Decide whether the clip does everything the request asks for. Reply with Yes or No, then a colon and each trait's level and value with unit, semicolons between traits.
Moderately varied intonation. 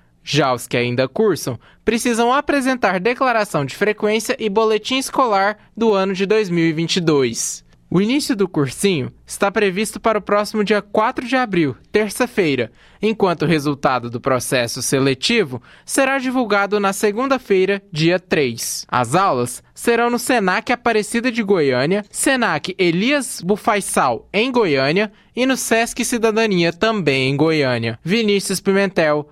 No: wide, 6.9 semitones